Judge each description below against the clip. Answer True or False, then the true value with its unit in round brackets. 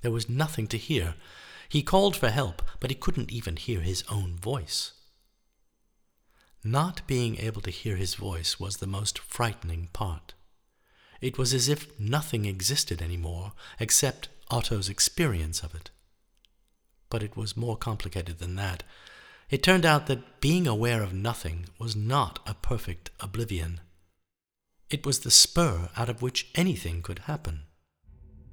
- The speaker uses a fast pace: False (150 wpm)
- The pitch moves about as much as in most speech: False (6.6 semitones)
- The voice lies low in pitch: True (105 Hz)